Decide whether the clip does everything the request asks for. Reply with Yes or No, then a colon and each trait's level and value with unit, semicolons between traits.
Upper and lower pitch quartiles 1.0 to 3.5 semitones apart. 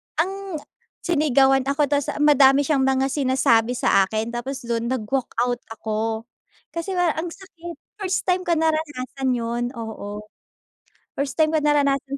No: average, 4.4 semitones